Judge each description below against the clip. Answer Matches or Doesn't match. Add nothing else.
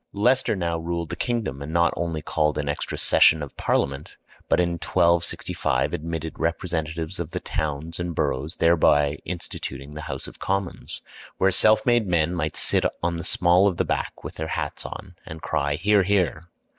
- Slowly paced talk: Doesn't match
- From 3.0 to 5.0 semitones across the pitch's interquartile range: Doesn't match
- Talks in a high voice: Doesn't match